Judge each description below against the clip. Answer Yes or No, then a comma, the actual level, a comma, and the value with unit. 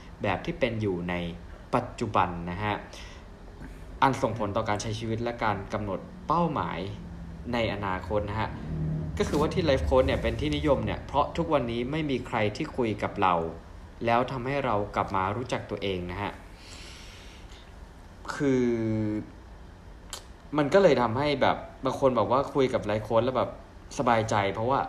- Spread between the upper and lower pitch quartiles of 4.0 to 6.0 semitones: Yes, average, 5.3 semitones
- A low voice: Yes, low, 105 Hz